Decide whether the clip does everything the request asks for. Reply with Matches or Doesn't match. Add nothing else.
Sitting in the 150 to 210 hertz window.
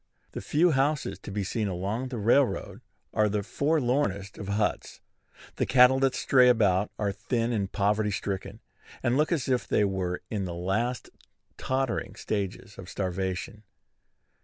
Doesn't match